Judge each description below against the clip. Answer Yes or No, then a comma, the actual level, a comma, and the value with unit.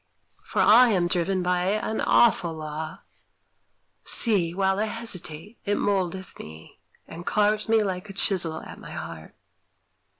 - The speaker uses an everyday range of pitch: Yes, average, 3.9 semitones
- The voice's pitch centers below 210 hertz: Yes, high, 190 Hz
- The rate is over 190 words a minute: No, average, 140 wpm